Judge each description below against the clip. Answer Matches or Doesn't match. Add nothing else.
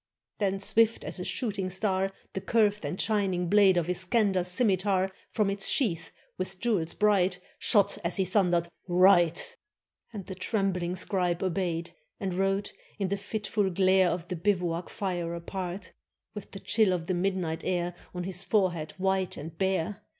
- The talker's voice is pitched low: Doesn't match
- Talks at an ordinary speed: Matches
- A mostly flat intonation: Matches